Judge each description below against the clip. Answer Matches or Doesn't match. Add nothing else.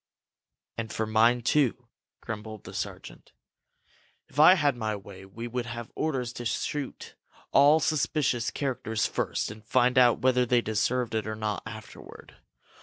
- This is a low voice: Matches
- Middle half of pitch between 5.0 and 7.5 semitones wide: Doesn't match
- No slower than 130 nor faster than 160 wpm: Matches